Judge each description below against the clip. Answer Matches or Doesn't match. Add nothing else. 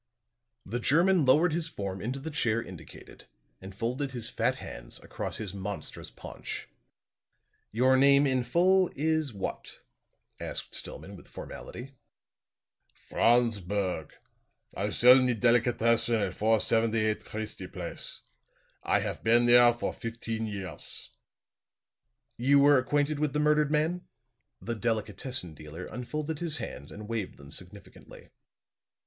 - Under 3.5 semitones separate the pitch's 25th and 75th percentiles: Doesn't match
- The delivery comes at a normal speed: Doesn't match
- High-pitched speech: Doesn't match